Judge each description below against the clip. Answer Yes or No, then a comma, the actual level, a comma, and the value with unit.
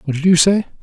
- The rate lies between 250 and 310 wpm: Yes, fast, 290 wpm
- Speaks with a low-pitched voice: No, medium, 170 Hz